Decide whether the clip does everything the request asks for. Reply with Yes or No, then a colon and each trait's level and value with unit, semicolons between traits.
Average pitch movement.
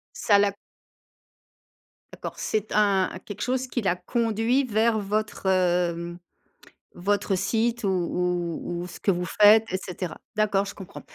Yes: average, 3.2 semitones